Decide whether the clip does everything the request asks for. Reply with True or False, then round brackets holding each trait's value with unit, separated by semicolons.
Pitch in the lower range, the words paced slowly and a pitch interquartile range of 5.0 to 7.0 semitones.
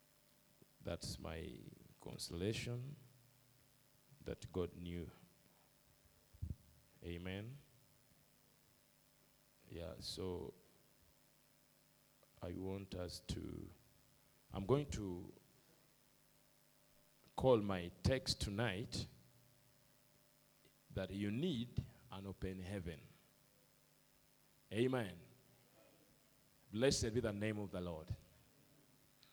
True (105 Hz; 70 wpm; 5.3 semitones)